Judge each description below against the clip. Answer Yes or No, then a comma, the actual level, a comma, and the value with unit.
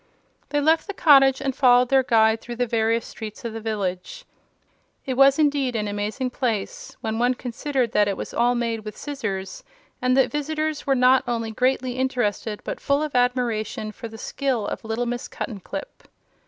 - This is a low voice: No, high, 245 Hz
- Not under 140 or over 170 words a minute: No, average, 180 wpm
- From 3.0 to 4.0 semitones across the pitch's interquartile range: Yes, average, 3.5 semitones